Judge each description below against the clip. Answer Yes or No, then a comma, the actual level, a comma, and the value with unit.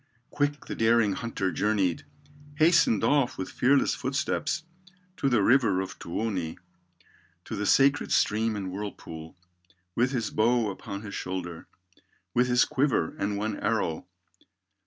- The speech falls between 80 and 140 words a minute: Yes, slow, 135 wpm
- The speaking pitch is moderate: No, low, 110 Hz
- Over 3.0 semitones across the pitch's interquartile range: Yes, average, 4.7 semitones